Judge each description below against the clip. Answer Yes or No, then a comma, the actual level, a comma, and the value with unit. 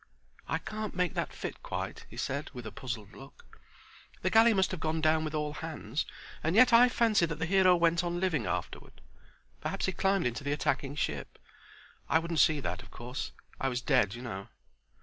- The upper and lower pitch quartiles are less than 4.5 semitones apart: No, wide, 5.4 semitones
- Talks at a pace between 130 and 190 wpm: No, average, 200 wpm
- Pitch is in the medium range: Yes, medium, 155 Hz